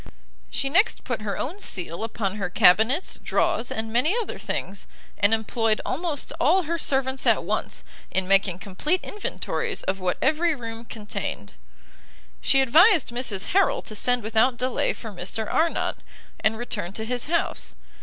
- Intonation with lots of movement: Yes, wide, 6.3 semitones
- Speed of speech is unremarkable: Yes, average, 155 wpm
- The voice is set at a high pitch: Yes, high, 230 Hz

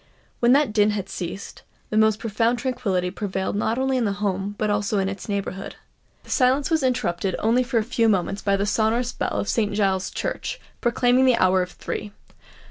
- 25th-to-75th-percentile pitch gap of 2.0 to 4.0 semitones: Yes, average, 3.7 semitones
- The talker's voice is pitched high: Yes, high, 210 Hz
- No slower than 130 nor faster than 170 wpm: No, average, 200 wpm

